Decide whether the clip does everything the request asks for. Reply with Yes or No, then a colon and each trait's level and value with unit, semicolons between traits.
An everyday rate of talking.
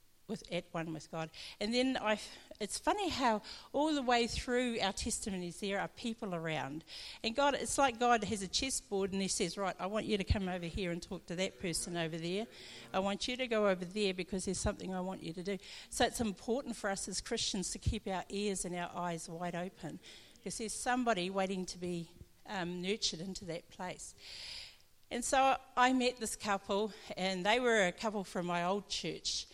No: fast, 215 wpm